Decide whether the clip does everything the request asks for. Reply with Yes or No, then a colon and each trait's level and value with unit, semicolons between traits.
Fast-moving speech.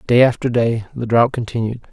No: average, 190 wpm